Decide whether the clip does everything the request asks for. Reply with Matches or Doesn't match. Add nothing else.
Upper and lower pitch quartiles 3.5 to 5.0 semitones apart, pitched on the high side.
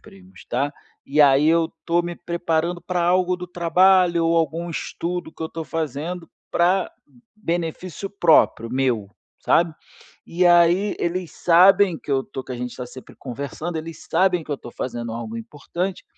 Doesn't match